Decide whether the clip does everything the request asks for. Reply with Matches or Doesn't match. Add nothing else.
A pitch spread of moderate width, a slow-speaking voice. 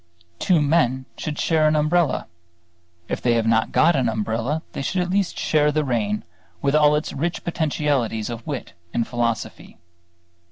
Doesn't match